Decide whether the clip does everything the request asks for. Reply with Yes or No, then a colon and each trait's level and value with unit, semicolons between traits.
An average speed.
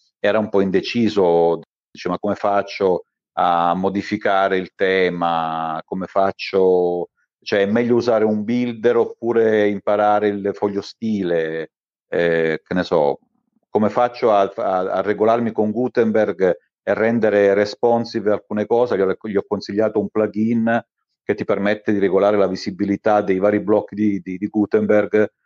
Yes: average, 150 wpm